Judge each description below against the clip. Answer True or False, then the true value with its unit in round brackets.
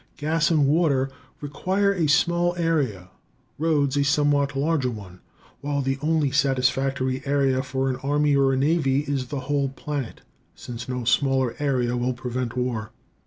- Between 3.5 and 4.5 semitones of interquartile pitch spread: False (2.4 semitones)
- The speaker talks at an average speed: True (155 wpm)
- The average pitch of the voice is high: False (140 Hz)